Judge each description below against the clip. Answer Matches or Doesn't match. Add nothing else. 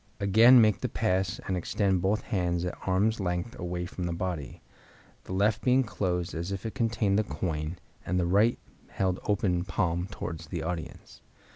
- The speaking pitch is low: Matches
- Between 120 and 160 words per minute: Doesn't match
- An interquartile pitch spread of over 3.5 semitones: Doesn't match